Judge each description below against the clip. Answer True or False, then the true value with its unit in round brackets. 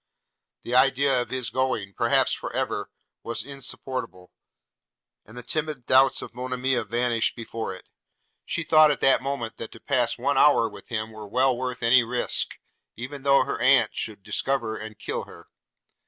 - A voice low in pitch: True (125 Hz)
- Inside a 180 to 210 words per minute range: False (170 wpm)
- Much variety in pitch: False (2.8 semitones)